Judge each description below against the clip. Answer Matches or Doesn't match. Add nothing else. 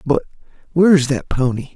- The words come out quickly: Doesn't match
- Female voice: Doesn't match